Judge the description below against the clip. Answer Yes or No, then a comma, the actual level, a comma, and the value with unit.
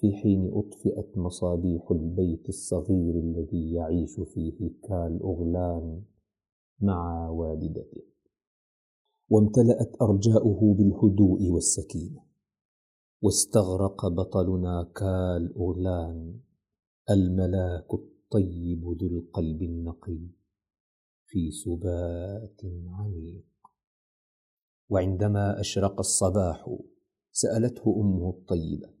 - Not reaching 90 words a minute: Yes, average, 70 wpm